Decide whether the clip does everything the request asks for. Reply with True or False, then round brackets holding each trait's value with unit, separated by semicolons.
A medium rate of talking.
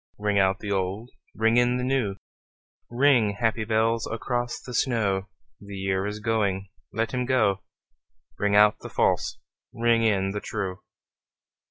True (150 wpm)